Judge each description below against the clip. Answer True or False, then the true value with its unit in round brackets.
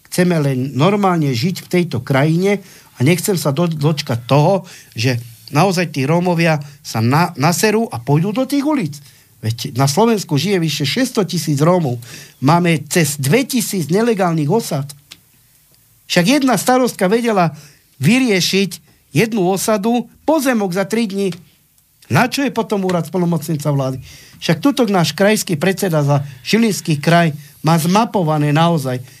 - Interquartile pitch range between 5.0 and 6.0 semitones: True (5.5 semitones)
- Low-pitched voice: False (170 Hz)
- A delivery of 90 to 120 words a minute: False (140 wpm)